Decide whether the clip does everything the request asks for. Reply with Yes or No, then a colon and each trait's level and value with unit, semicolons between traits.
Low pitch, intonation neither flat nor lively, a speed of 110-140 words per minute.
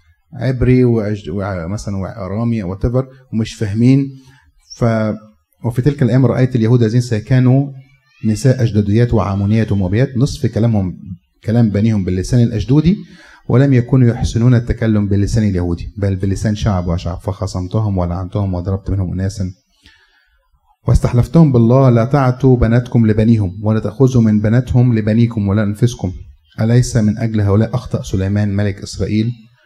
Yes: low, 110 Hz; average, 3.7 semitones; average, 125 wpm